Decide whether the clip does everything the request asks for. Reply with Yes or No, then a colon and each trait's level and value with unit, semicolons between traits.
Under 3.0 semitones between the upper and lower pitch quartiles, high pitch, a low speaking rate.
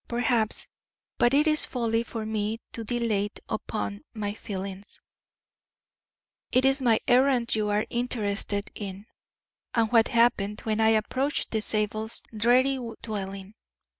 Yes: narrow, 2.6 semitones; high, 220 Hz; slow, 130 wpm